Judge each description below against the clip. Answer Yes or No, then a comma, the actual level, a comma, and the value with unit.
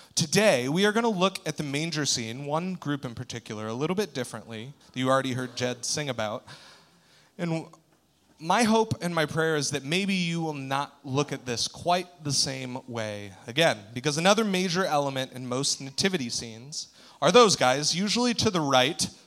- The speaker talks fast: No, average, 185 wpm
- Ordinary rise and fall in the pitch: No, wide, 5.8 semitones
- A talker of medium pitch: Yes, medium, 145 Hz